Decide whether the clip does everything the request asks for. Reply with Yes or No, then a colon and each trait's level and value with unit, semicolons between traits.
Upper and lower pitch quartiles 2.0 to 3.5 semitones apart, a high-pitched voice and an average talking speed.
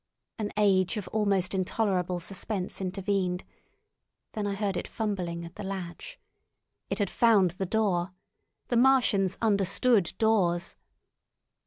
No: average, 2.7 semitones; high, 195 Hz; slow, 125 wpm